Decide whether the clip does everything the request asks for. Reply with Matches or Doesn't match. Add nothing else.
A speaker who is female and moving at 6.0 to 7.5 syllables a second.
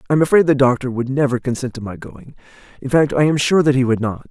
Doesn't match